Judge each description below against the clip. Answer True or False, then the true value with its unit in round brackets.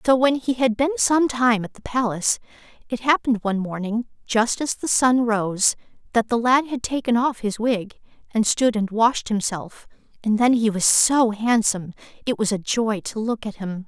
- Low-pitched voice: False (230 Hz)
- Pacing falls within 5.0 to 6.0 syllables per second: False (4.8 syllables/s)